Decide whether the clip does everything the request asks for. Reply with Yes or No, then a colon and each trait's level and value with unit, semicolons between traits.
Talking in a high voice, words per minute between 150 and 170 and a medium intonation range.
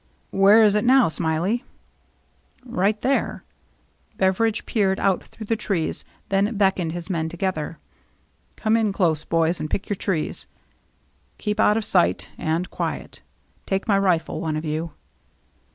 Yes: high, 195 Hz; average, 160 wpm; average, 4.3 semitones